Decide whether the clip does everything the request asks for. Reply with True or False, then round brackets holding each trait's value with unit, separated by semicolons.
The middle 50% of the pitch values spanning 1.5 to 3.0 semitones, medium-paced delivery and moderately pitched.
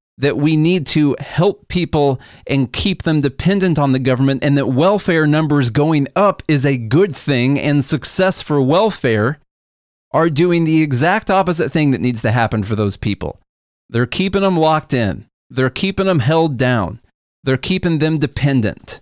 False (4.4 semitones; 170 wpm; 145 Hz)